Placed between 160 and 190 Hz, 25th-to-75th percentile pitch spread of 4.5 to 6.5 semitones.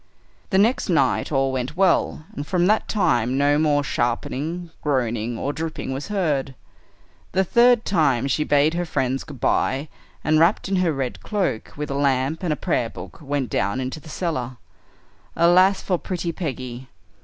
No: medium, 145 Hz; average, 4.8 semitones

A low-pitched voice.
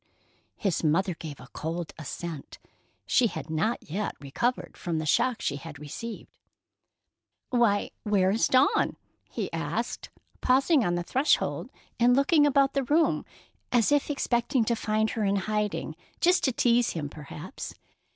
No: high, 215 Hz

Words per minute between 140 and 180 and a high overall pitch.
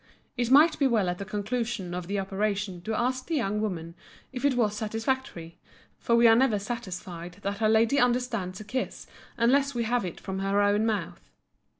No: average, 195 wpm; high, 215 Hz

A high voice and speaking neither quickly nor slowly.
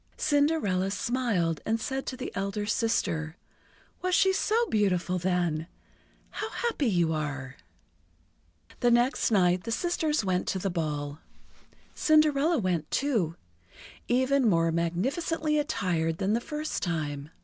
No: high, 205 Hz; slow, 125 wpm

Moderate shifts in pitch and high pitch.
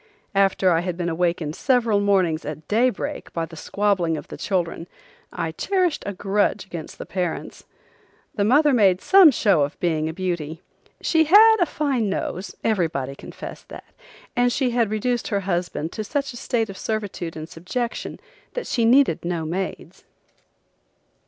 No: wide, 6.1 semitones; high, 195 Hz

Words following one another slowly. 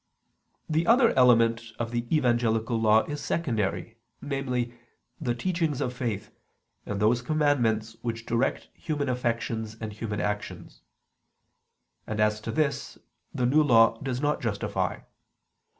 Yes: slow, 130 wpm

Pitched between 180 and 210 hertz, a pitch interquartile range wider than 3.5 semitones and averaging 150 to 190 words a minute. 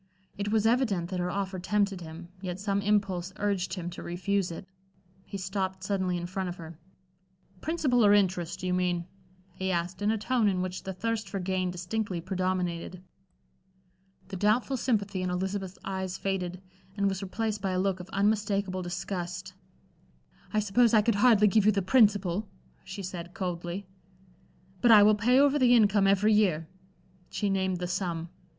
No: high, 190 Hz; narrow, 2.4 semitones; average, 175 wpm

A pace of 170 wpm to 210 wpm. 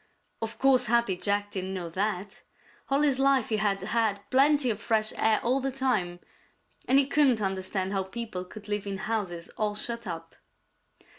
Yes: average, 175 wpm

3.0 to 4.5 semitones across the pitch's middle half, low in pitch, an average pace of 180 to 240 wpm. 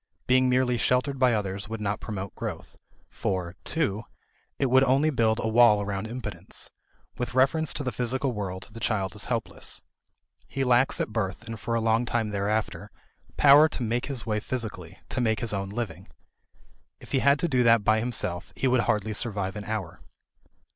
Yes: average, 3.6 semitones; low, 115 Hz; average, 185 wpm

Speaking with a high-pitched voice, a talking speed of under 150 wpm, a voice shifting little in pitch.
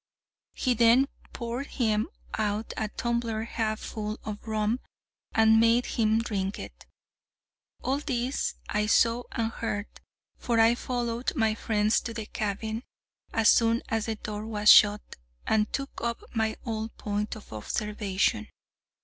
Yes: high, 220 Hz; average, 140 wpm; narrow, 1.7 semitones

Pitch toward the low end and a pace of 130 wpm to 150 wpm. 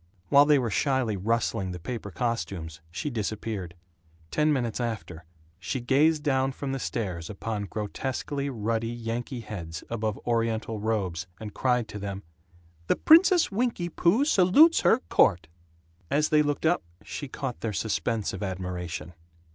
Yes: low, 115 Hz; average, 145 wpm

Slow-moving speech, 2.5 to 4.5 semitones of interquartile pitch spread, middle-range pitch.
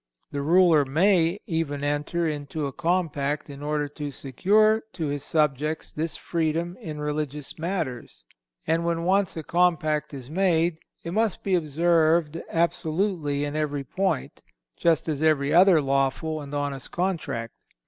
No: average, 145 wpm; average, 2.8 semitones; medium, 155 Hz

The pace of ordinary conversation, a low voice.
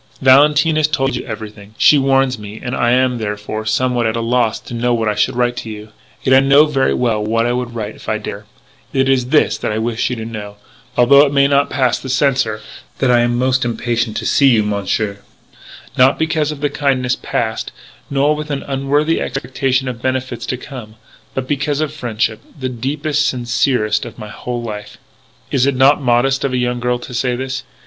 No: fast, 210 wpm; low, 125 Hz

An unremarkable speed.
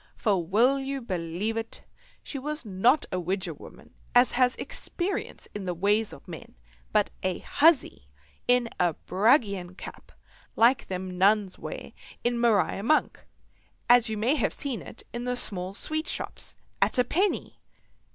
Yes: average, 160 wpm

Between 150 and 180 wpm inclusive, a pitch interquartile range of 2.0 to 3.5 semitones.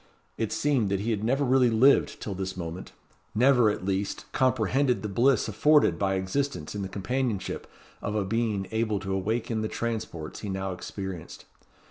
No: average, 170 wpm; average, 4.4 semitones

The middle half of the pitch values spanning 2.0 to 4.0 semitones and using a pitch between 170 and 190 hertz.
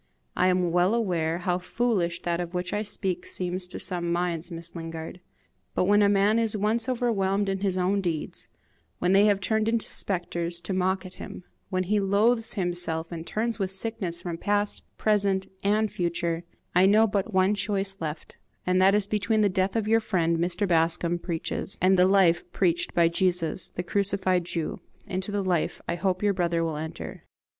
Yes: average, 2.8 semitones; medium, 185 Hz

